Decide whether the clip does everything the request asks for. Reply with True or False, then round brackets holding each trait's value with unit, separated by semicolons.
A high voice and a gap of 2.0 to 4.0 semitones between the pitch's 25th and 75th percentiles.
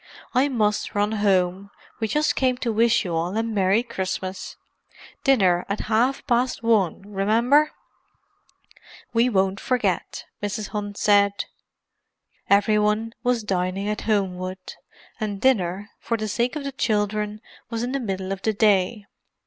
True (210 Hz; 3.0 semitones)